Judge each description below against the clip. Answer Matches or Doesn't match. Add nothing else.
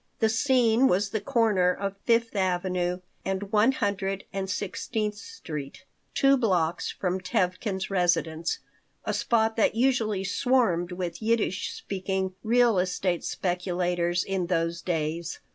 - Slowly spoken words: Matches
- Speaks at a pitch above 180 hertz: Matches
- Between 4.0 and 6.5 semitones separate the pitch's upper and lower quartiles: Doesn't match